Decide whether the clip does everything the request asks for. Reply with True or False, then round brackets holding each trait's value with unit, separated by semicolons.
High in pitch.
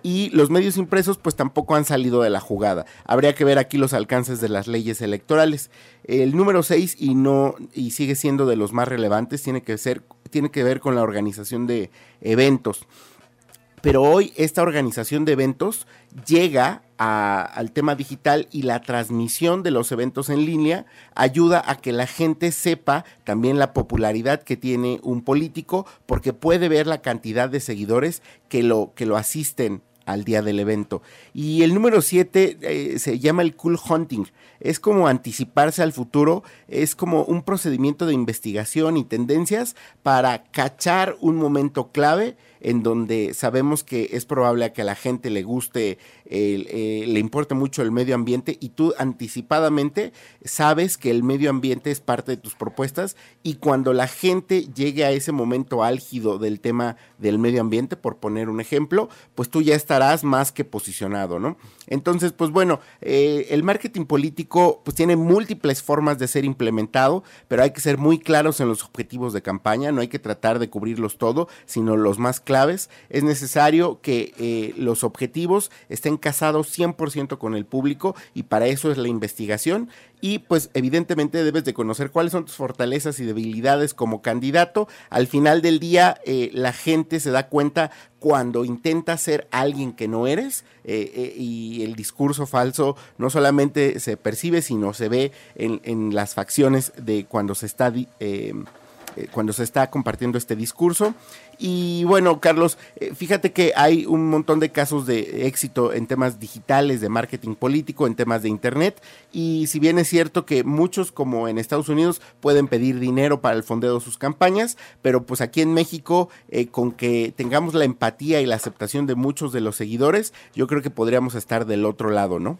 False (135 Hz)